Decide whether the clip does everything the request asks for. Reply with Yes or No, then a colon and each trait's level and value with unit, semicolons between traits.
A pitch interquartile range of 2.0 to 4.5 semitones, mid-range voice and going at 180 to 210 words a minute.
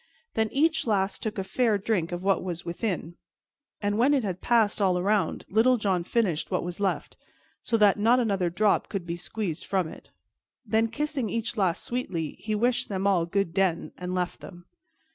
No: average, 3.9 semitones; high, 200 Hz; average, 190 wpm